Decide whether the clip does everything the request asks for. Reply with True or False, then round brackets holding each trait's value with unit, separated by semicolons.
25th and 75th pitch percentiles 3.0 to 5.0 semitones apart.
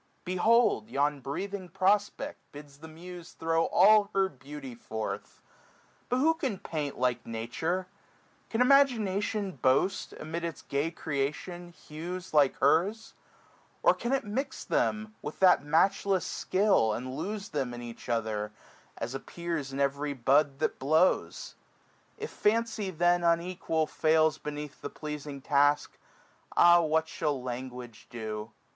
False (5.6 semitones)